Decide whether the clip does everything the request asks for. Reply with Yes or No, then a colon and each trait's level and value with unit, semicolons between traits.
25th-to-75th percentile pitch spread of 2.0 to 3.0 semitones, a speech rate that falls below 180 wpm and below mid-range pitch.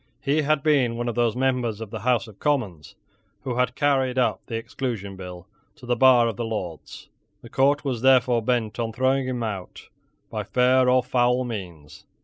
No: average, 2.7 semitones; average, 190 wpm; low, 120 Hz